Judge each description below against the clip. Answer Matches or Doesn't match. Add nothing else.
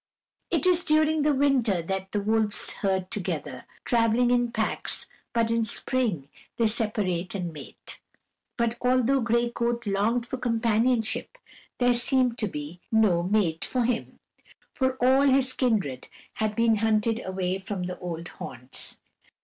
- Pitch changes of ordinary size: Matches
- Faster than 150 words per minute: Doesn't match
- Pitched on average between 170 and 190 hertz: Doesn't match